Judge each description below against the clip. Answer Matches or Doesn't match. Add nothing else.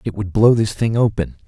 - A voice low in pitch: Matches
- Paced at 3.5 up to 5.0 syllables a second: Doesn't match